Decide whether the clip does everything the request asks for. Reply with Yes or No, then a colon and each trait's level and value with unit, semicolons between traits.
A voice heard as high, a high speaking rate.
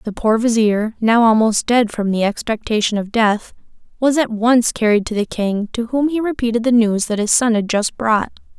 Yes: high, 225 Hz; fast, 210 wpm